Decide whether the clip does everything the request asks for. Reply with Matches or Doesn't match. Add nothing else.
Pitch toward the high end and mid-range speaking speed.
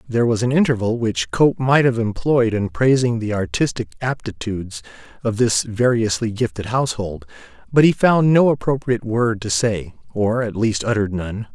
Doesn't match